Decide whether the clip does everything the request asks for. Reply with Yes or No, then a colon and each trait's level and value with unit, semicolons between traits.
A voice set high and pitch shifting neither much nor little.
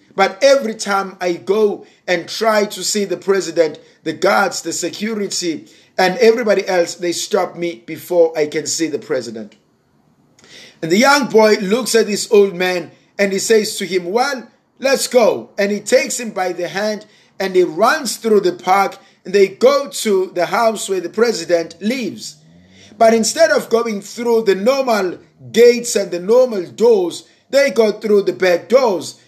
Yes: high, 200 Hz; average, 4.3 semitones